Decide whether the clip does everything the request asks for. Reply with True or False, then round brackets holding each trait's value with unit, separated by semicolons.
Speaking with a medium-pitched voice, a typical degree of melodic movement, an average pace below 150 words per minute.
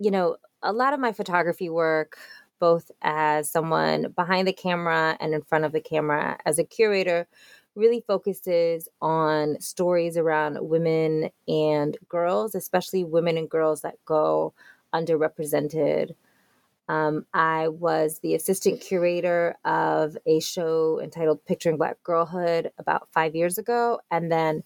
False (165 Hz; 2.2 semitones; 140 wpm)